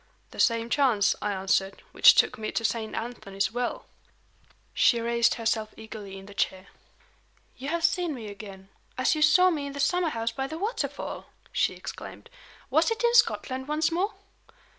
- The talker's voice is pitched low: No, high, 240 Hz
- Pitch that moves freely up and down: Yes, wide, 6.5 semitones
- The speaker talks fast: No, average, 175 wpm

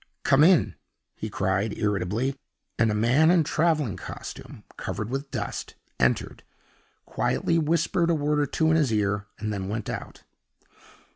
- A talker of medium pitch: No, low, 125 Hz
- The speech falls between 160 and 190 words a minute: No, average, 150 wpm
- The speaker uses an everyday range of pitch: No, wide, 7.0 semitones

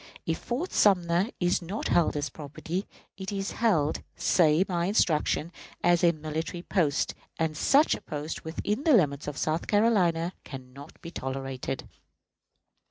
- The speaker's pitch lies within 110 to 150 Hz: No, medium, 170 Hz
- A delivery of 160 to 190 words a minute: No, average, 150 wpm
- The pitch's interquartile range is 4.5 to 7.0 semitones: No, average, 4.1 semitones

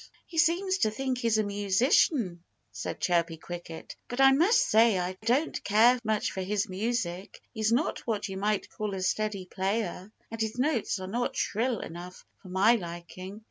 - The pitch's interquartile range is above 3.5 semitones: Yes, average, 4.3 semitones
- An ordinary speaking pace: Yes, average, 180 wpm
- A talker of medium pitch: No, high, 215 Hz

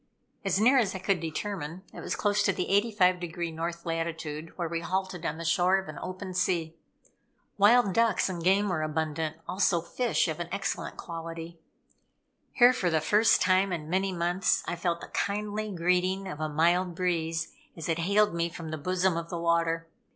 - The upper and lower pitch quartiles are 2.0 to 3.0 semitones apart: Yes, narrow, 2.6 semitones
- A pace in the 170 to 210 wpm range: Yes, average, 190 wpm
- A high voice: No, medium, 175 Hz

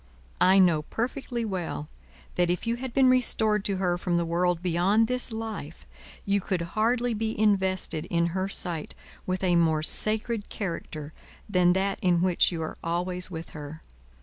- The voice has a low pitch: No, medium, 185 Hz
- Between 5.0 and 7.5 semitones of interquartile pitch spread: No, average, 4.0 semitones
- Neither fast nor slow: Yes, average, 170 wpm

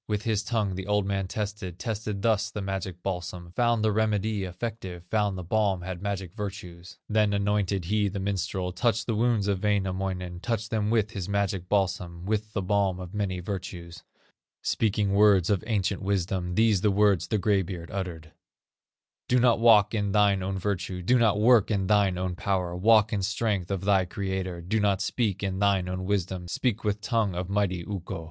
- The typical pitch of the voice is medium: No, low, 100 Hz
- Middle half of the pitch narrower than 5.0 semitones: Yes, narrow, 2.4 semitones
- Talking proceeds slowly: No, average, 190 wpm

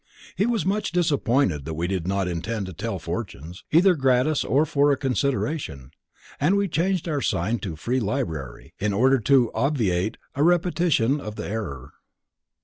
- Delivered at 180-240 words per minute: No, average, 165 wpm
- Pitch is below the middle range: Yes, low, 130 Hz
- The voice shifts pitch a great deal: Yes, wide, 8.3 semitones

